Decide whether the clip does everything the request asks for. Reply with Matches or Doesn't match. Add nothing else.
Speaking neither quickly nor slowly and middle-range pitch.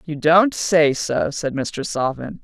Matches